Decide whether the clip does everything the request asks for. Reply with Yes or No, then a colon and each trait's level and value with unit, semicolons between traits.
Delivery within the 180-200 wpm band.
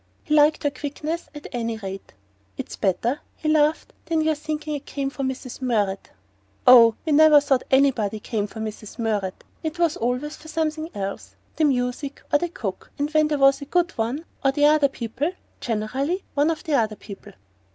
Yes: average, 185 wpm